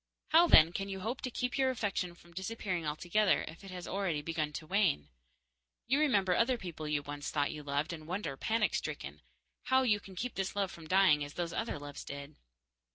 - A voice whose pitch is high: No, medium, 180 Hz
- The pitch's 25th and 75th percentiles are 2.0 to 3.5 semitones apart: No, wide, 5.5 semitones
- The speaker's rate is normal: No, fast, 210 wpm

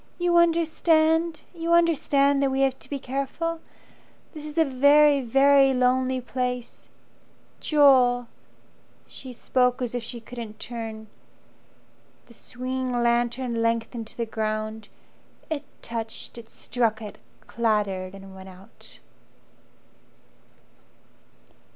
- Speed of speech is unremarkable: No, slow, 115 wpm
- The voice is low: No, very high, 250 Hz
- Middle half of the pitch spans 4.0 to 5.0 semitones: No, average, 3.6 semitones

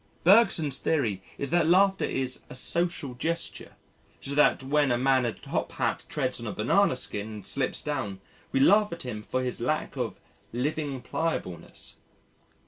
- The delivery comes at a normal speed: Yes, average, 170 wpm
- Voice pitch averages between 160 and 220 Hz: No, low, 135 Hz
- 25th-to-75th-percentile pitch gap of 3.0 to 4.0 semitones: No, average, 5.0 semitones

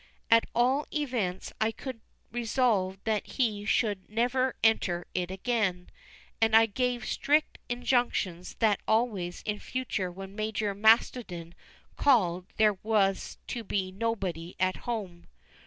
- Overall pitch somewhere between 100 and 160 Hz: No, high, 215 Hz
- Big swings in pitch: No, average, 4.2 semitones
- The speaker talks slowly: Yes, slow, 125 wpm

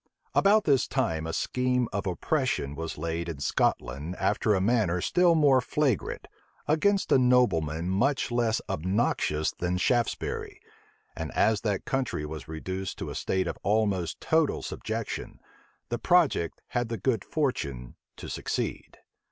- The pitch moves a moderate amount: No, wide, 7.5 semitones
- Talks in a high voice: No, low, 105 Hz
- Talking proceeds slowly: No, average, 145 wpm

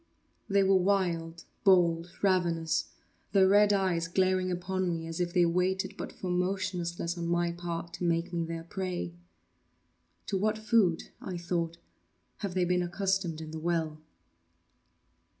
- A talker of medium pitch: Yes, medium, 175 Hz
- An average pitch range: No, narrow, 2.1 semitones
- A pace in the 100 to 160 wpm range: Yes, average, 145 wpm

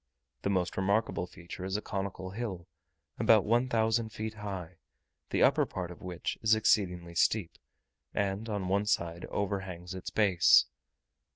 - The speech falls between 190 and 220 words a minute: No, average, 150 wpm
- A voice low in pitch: Yes, very low, 95 Hz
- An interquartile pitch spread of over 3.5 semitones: No, average, 3.0 semitones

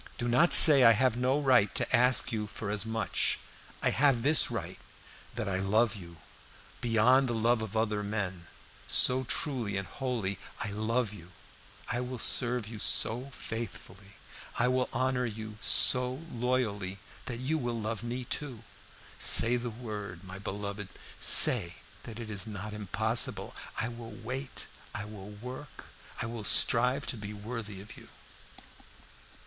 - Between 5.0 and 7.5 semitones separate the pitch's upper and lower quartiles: No, average, 3.4 semitones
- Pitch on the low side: Yes, low, 115 Hz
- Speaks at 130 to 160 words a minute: Yes, average, 155 wpm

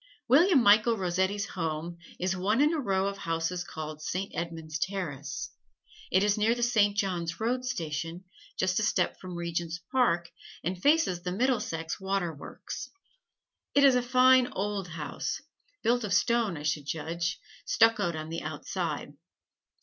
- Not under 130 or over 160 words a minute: Yes, average, 150 wpm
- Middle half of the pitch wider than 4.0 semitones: Yes, average, 5.2 semitones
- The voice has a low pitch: No, medium, 185 Hz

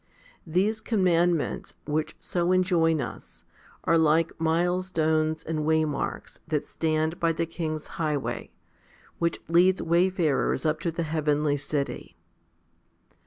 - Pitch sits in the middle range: Yes, medium, 160 Hz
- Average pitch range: No, narrow, 1.9 semitones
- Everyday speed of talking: No, slow, 120 wpm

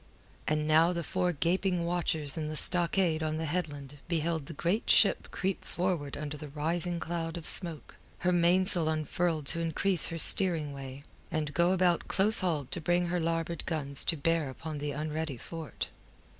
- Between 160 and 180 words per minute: Yes, average, 175 wpm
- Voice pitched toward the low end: No, medium, 165 Hz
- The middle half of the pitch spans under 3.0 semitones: Yes, narrow, 2.5 semitones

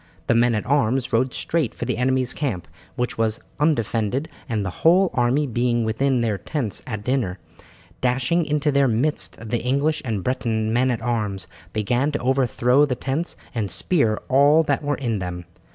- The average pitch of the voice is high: No, low, 125 Hz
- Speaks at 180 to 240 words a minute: No, average, 170 wpm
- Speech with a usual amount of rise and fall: Yes, average, 3.9 semitones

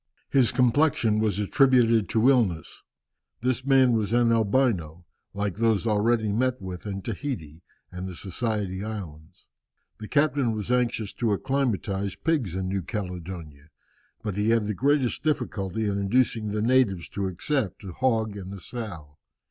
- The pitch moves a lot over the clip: No, average, 4.5 semitones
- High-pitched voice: No, low, 110 Hz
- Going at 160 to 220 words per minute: No, average, 150 wpm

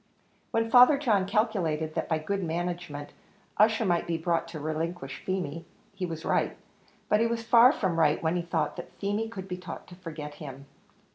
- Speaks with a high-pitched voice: No, medium, 175 Hz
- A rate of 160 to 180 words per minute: No, average, 190 wpm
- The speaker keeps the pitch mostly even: No, average, 4.6 semitones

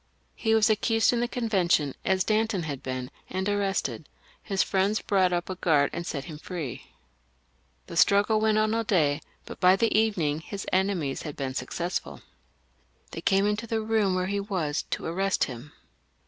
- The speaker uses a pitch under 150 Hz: No, high, 190 Hz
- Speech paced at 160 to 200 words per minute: Yes, average, 180 wpm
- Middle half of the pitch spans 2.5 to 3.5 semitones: No, average, 5.0 semitones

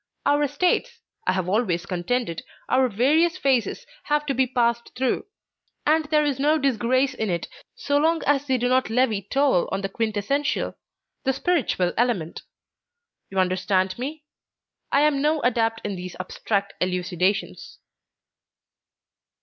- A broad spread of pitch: Yes, wide, 6.6 semitones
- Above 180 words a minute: No, average, 140 wpm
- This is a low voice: No, very high, 250 Hz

